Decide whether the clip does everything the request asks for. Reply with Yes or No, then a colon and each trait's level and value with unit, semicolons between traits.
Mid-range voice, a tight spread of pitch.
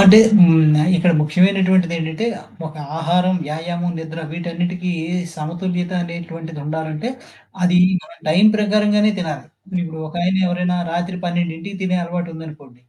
Yes: medium, 175 Hz; narrow, 2.0 semitones